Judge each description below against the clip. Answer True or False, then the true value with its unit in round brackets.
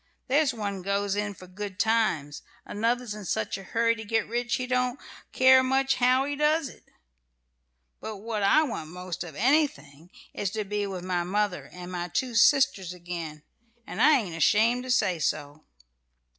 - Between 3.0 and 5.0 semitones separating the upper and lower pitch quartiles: False (5.6 semitones)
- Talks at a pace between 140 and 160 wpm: False (175 wpm)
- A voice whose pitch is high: True (210 Hz)